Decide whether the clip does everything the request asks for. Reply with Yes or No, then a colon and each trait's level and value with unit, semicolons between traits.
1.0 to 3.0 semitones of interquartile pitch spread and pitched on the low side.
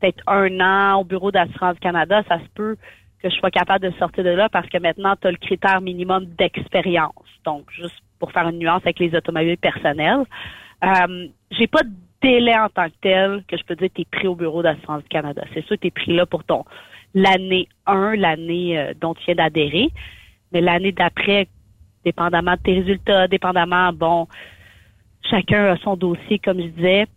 No: narrow, 2.4 semitones; medium, 180 Hz